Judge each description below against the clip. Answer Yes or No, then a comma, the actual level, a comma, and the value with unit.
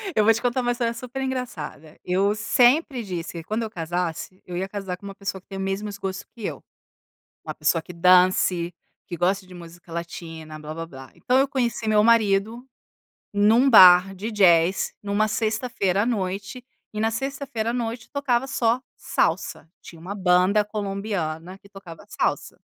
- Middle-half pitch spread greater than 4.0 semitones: Yes, average, 4.4 semitones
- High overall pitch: Yes, high, 200 Hz